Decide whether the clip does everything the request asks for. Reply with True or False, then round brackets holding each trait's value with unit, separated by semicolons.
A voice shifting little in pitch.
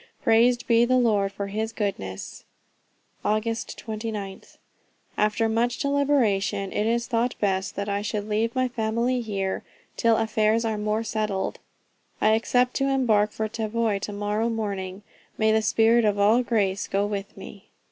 True (2.2 semitones)